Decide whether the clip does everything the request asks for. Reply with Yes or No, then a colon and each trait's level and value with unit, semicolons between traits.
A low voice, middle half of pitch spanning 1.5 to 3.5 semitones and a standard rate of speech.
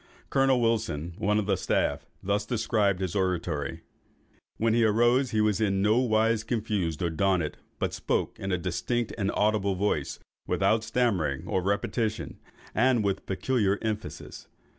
Yes: low, 105 Hz; average, 3.0 semitones; average, 145 wpm